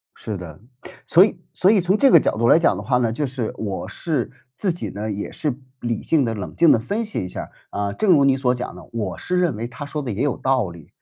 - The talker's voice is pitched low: Yes, low, 125 Hz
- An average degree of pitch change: No, wide, 7.3 semitones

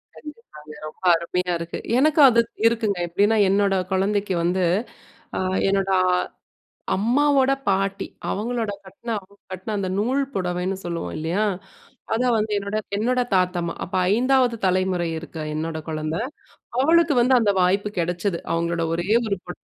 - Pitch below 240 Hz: Yes, high, 195 Hz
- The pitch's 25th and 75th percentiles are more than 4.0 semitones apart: Yes, average, 4.4 semitones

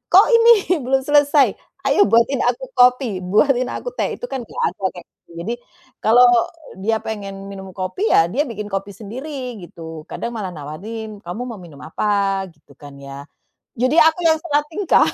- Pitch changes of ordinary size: No, wide, 5.8 semitones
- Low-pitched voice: No, high, 230 Hz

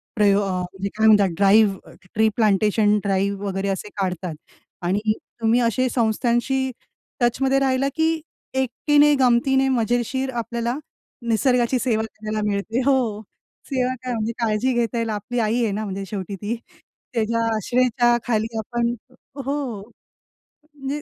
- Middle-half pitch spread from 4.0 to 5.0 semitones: No, average, 3.5 semitones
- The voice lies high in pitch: Yes, high, 230 Hz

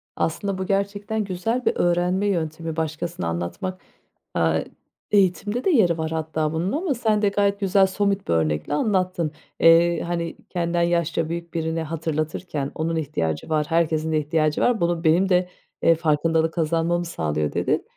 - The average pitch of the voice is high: No, medium, 170 Hz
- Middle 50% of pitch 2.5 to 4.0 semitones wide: Yes, average, 3.1 semitones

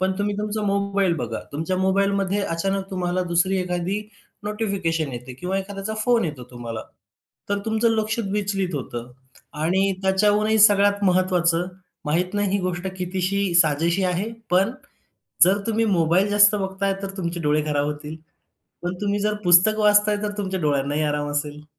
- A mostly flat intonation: No, average, 3.4 semitones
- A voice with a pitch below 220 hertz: Yes, high, 190 Hz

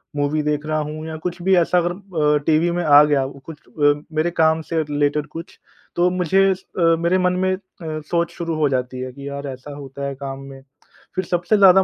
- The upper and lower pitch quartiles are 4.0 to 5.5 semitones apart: No, average, 3.2 semitones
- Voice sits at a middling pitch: Yes, medium, 155 Hz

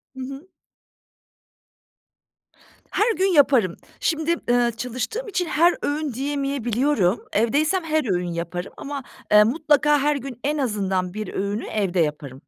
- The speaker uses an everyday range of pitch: No, wide, 6.4 semitones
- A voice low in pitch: No, very high, 265 Hz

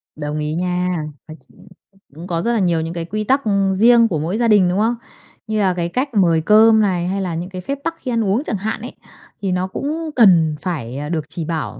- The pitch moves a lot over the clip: No, average, 4.8 semitones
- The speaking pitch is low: No, medium, 185 Hz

